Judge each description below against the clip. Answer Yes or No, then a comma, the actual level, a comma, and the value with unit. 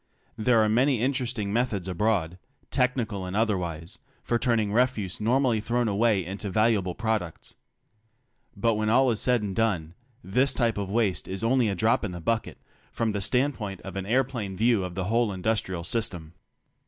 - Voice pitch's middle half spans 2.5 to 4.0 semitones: Yes, average, 3.6 semitones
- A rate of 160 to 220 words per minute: Yes, average, 175 wpm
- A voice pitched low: Yes, low, 110 Hz